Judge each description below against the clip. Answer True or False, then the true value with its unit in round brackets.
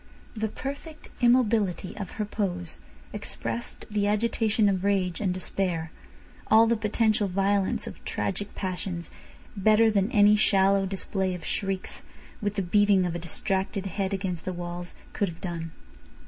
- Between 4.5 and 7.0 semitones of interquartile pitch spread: False (2.5 semitones)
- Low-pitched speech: False (195 Hz)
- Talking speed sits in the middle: True (145 wpm)